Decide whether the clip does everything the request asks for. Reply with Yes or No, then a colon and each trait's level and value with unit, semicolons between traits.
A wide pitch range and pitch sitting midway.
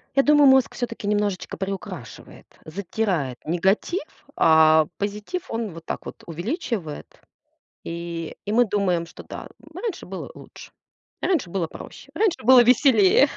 No: wide, 7.4 semitones; high, 205 Hz